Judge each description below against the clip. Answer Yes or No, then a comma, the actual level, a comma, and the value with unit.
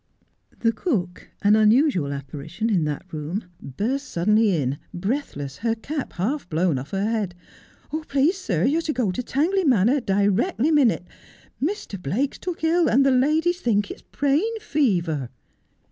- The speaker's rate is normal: Yes, average, 160 wpm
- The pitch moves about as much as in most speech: No, wide, 8.2 semitones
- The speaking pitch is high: Yes, high, 225 Hz